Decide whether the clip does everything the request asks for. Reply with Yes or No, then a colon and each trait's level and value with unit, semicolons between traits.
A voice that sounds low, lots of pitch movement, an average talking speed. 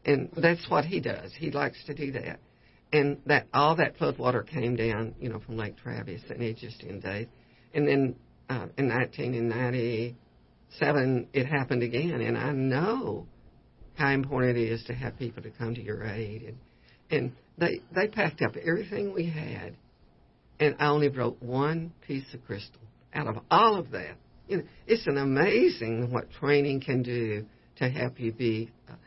No: low, 120 Hz; average, 3.3 semitones; average, 180 wpm